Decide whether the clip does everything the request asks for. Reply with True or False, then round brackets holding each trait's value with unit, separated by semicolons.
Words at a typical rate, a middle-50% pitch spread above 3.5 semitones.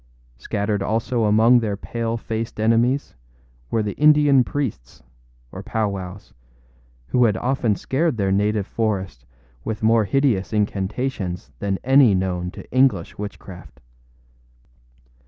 False (120 wpm; 3.9 semitones)